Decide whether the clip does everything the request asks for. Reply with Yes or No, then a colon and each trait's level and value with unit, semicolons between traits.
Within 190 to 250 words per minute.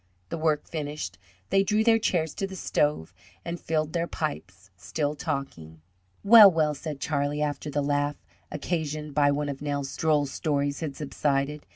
No: average, 165 wpm